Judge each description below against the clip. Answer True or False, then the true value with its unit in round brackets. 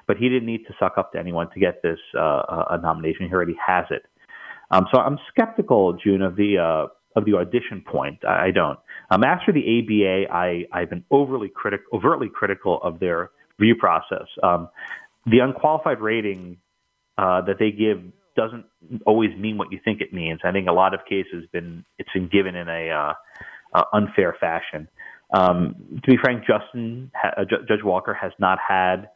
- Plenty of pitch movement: False (4.1 semitones)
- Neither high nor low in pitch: False (100 Hz)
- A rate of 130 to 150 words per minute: False (190 wpm)